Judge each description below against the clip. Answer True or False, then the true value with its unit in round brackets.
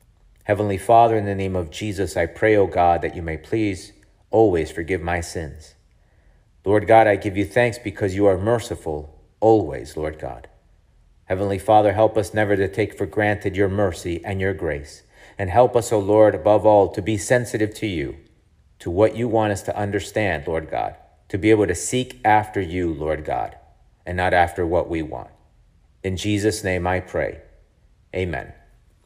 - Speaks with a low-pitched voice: True (100 Hz)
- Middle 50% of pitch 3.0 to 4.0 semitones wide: True (3.3 semitones)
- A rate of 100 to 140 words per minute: False (180 wpm)